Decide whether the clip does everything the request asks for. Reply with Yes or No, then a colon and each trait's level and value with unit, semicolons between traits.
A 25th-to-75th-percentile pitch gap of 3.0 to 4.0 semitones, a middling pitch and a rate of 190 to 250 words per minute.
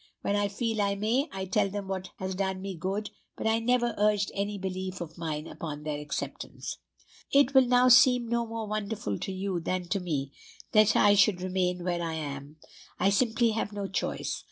No: average, 3.4 semitones; high, 195 Hz; average, 200 wpm